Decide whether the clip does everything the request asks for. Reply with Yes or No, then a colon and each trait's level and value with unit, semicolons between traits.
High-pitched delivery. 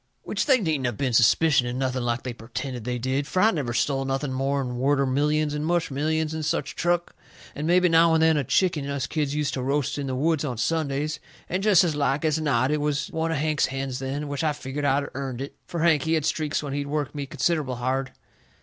No: medium, 145 Hz